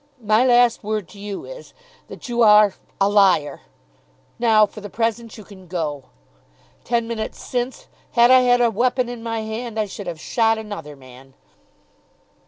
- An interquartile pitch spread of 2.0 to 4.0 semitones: Yes, average, 3.0 semitones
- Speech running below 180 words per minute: Yes, average, 170 wpm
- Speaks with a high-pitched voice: Yes, high, 220 Hz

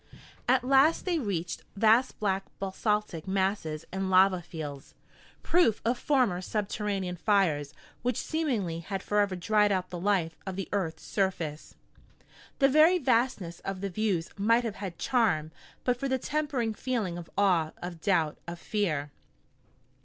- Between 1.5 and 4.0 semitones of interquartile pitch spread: No, average, 4.8 semitones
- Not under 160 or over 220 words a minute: No, average, 145 wpm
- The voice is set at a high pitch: Yes, high, 195 Hz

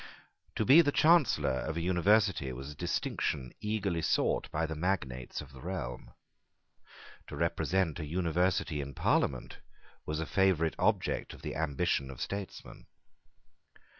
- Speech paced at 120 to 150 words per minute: Yes, average, 140 wpm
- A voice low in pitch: Yes, very low, 80 Hz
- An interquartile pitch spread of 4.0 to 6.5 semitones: Yes, average, 5.3 semitones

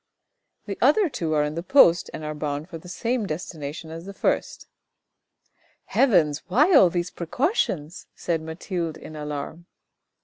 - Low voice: No, medium, 170 Hz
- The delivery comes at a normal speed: Yes, average, 165 wpm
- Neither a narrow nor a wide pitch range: Yes, average, 3.9 semitones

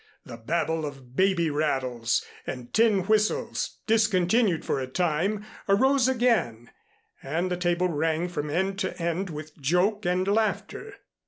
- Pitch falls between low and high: Yes, medium, 175 Hz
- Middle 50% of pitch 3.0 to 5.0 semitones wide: No, wide, 5.4 semitones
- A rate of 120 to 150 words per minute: Yes, average, 140 wpm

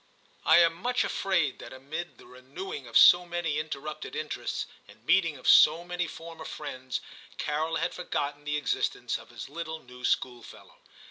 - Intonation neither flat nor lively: Yes, average, 3.5 semitones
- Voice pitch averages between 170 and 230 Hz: No, medium, 155 Hz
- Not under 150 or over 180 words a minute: Yes, average, 160 wpm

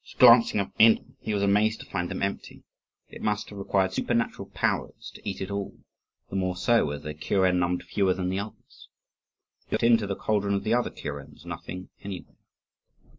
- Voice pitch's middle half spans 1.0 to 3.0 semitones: Yes, narrow, 2.6 semitones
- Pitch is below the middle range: Yes, low, 100 Hz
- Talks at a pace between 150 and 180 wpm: No, average, 190 wpm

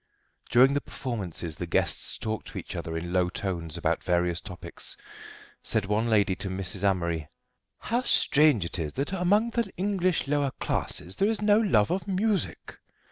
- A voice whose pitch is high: No, low, 110 Hz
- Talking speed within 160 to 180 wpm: Yes, average, 170 wpm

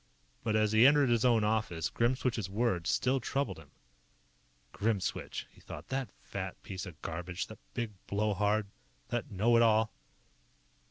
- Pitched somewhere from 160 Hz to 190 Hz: No, low, 110 Hz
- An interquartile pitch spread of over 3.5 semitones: No, average, 3.2 semitones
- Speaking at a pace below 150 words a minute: No, average, 155 wpm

